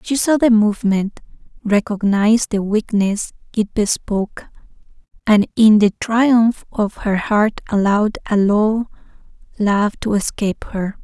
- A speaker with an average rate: No, slow, 125 wpm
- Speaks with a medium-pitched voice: No, high, 210 Hz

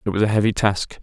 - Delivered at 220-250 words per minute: No, fast, 295 wpm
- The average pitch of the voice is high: No, low, 105 Hz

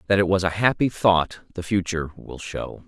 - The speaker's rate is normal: No, fast, 210 wpm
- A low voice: Yes, very low, 90 Hz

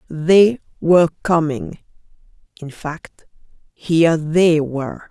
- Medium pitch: Yes, medium, 160 Hz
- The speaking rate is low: Yes, slow, 80 wpm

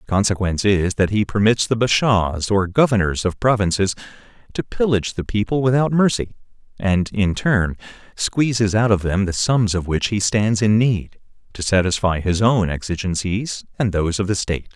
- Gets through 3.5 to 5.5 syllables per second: Yes, 5.2 syllables/s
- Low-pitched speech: Yes, low, 105 Hz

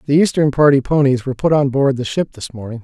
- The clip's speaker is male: Yes, male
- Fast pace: Yes, fast, 255 wpm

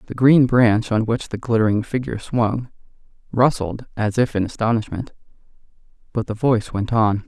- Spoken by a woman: No, male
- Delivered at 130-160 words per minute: Yes, average, 155 wpm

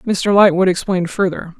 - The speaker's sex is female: Yes, female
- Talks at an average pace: Yes, average, 150 wpm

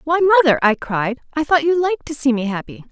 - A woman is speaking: Yes, female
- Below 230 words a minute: No, fast, 245 wpm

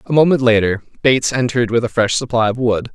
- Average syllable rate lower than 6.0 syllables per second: No, 6.5 syllables/s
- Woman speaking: No, male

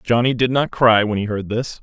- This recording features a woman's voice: No, male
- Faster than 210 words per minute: Yes, fast, 265 wpm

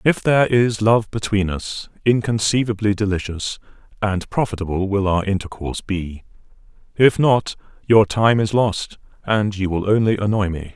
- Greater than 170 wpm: No, average, 145 wpm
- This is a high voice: No, low, 105 Hz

